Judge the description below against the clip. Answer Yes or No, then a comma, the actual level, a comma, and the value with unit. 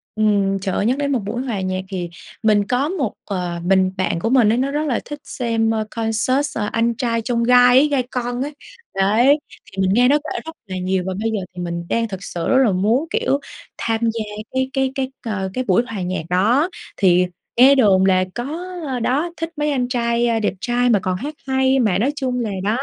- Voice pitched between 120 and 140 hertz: No, high, 230 Hz